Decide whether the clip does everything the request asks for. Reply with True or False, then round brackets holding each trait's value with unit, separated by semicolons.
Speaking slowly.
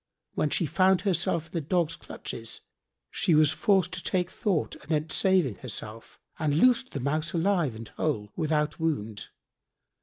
False (155 wpm)